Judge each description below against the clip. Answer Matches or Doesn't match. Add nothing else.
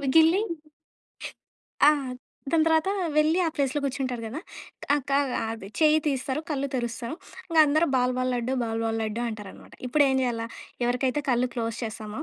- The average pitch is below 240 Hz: Doesn't match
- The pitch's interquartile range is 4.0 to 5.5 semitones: Matches